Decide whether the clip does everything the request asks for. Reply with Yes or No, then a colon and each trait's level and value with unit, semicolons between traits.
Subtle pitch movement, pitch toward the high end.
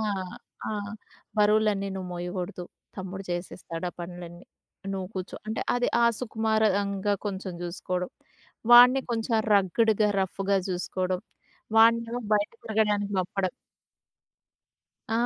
No: average, 3.1 semitones; high, 200 Hz